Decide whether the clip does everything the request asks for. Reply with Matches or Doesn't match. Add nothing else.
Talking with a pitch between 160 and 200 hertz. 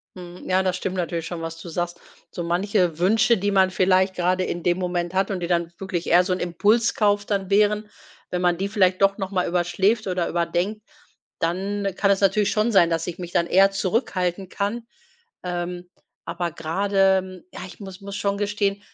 Matches